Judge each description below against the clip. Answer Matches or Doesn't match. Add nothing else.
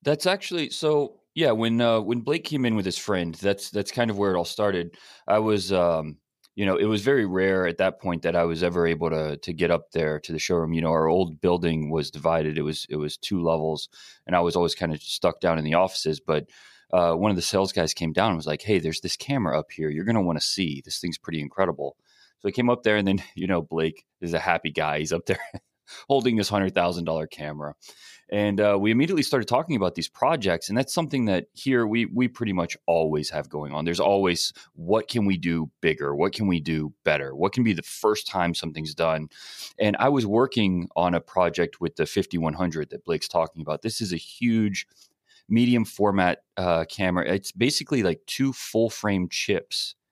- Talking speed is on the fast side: Matches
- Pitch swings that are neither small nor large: Matches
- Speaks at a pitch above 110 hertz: Doesn't match